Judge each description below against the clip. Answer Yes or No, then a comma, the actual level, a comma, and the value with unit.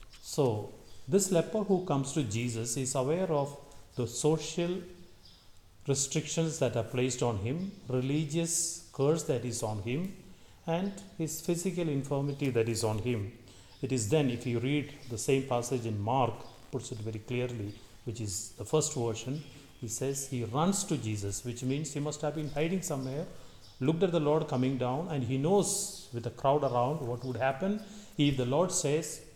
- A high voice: No, low, 135 Hz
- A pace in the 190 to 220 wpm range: No, average, 175 wpm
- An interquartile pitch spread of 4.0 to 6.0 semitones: Yes, average, 4.7 semitones